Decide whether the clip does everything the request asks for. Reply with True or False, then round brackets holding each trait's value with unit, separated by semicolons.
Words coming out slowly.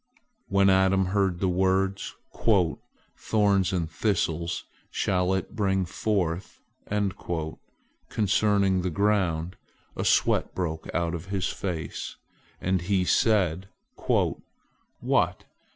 True (105 wpm)